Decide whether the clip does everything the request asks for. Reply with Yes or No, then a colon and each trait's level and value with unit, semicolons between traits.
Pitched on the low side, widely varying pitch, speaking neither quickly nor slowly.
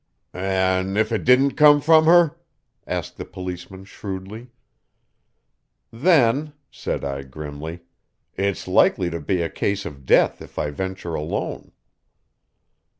No: very low, 95 Hz; wide, 6.4 semitones; slow, 125 wpm